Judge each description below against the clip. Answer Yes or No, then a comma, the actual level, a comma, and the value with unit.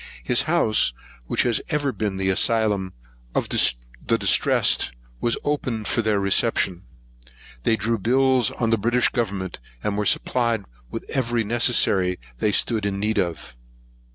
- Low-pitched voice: Yes, low, 110 Hz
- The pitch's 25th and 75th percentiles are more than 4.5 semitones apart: No, average, 3.6 semitones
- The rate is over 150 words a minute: No, average, 145 wpm